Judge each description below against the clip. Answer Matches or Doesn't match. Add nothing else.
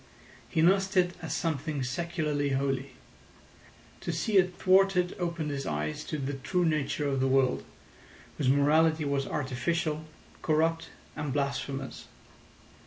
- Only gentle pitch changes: Doesn't match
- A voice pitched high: Doesn't match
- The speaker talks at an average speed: Doesn't match